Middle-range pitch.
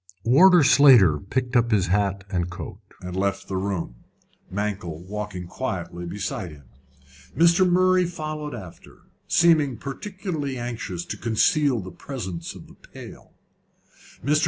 No: low, 110 Hz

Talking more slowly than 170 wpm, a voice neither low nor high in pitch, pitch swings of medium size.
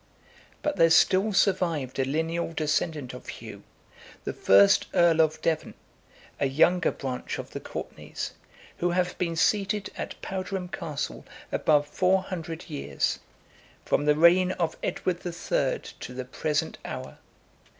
Yes: average, 140 wpm; medium, 165 Hz; average, 3.7 semitones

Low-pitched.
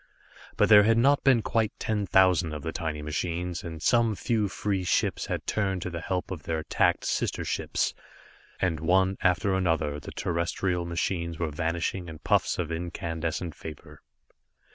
Yes: very low, 90 Hz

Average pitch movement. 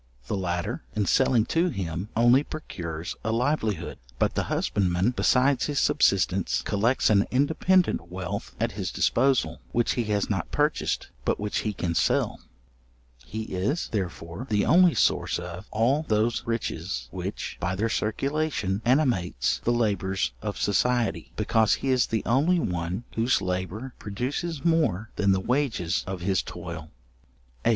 No: wide, 5.7 semitones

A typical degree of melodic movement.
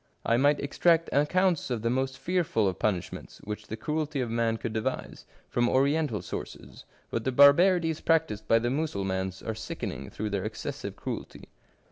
No: wide, 5.9 semitones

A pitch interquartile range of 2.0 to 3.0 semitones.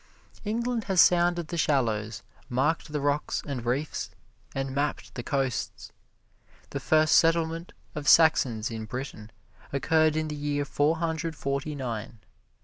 No: average, 3.6 semitones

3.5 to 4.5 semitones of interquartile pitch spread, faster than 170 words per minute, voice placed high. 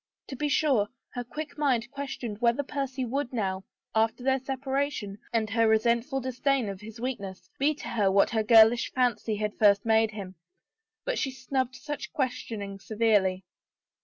No: average, 4.1 semitones; average, 165 wpm; high, 235 Hz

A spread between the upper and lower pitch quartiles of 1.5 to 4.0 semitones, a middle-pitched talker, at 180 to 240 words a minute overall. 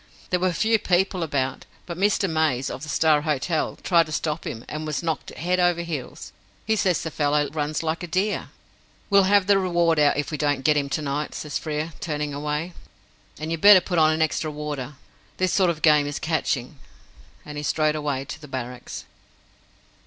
Yes: average, 2.8 semitones; medium, 155 Hz; average, 200 wpm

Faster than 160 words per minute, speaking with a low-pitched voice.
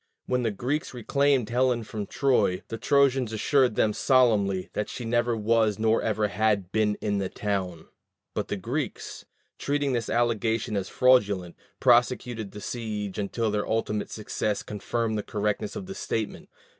No: average, 155 wpm; low, 110 Hz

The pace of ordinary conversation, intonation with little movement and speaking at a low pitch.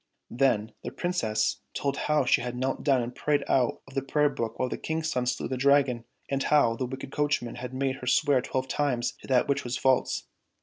No: fast, 220 wpm; narrow, 2.2 semitones; low, 130 Hz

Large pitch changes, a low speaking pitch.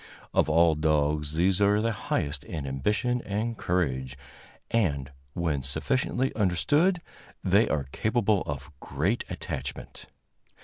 Yes: wide, 7.0 semitones; very low, 85 Hz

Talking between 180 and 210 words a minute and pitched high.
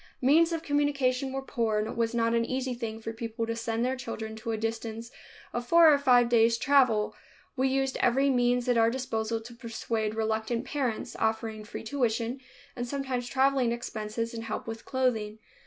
Yes: average, 190 wpm; high, 235 Hz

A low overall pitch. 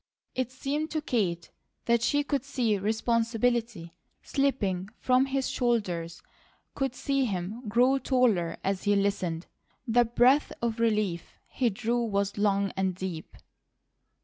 No: high, 230 Hz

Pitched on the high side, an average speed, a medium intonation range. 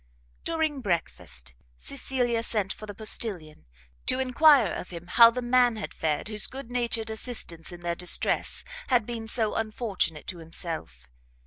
No: high, 220 Hz; average, 150 wpm; wide, 6.1 semitones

